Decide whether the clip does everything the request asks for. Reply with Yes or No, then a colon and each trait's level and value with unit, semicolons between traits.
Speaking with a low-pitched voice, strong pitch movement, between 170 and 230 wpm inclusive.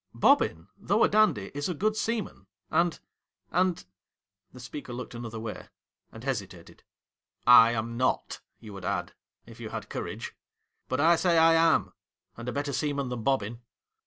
Yes: low, 125 Hz; wide, 6.5 semitones; average, 185 wpm